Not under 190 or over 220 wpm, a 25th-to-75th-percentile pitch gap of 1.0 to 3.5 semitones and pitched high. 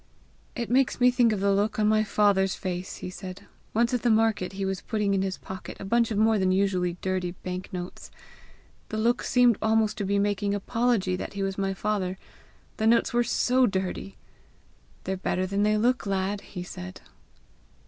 Yes: average, 200 wpm; average, 2.7 semitones; high, 200 Hz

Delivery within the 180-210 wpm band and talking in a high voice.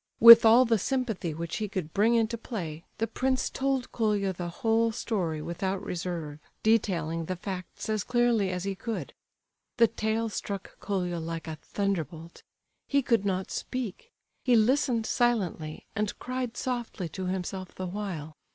No: average, 155 wpm; high, 200 Hz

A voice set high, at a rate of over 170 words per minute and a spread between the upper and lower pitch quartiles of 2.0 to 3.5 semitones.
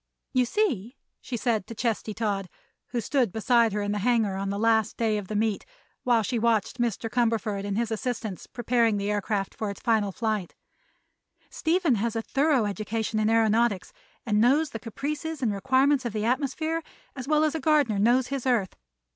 Yes: high, 230 Hz; average, 190 wpm; average, 3.2 semitones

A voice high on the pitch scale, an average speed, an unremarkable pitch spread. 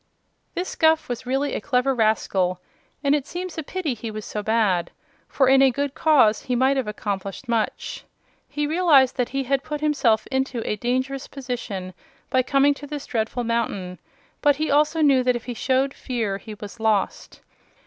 Yes: very high, 255 Hz; average, 185 wpm; average, 4.3 semitones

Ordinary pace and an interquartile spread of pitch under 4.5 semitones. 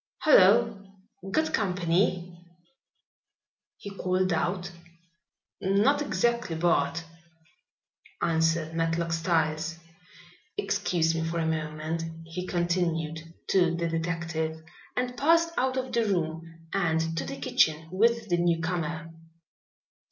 No: slow, 105 wpm; average, 3.2 semitones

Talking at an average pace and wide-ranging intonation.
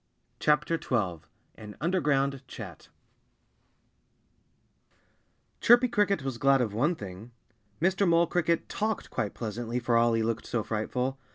No: slow, 120 wpm; wide, 6.7 semitones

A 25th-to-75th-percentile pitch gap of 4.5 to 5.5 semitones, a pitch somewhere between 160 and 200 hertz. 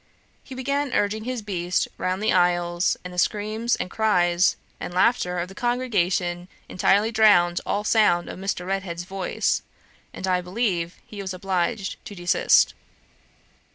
No: average, 3.5 semitones; high, 190 Hz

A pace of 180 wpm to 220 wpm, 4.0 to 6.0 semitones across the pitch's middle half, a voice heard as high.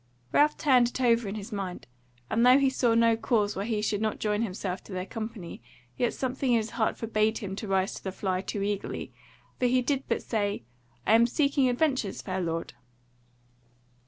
No: average, 200 wpm; average, 3.6 semitones; high, 220 Hz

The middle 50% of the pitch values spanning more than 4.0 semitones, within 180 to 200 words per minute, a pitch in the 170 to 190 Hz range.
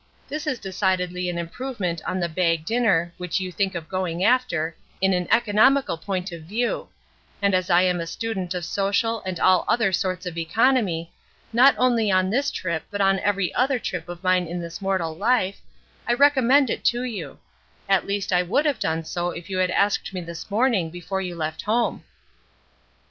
Yes: average, 4.5 semitones; average, 190 wpm; medium, 185 Hz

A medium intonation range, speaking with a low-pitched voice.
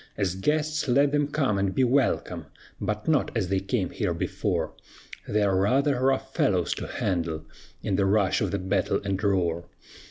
No: wide, 6.0 semitones; low, 100 Hz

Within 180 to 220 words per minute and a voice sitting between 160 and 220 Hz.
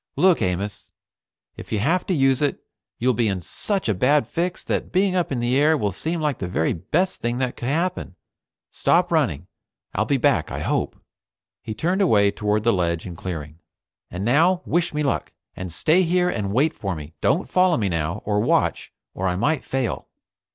No: average, 200 wpm; low, 120 Hz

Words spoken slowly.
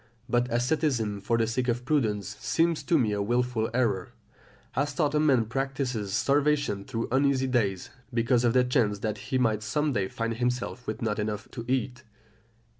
No: average, 180 wpm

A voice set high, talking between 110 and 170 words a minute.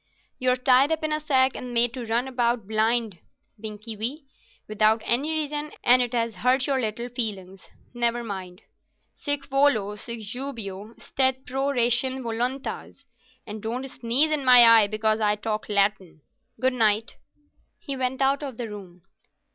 Yes: high, 240 Hz; average, 160 wpm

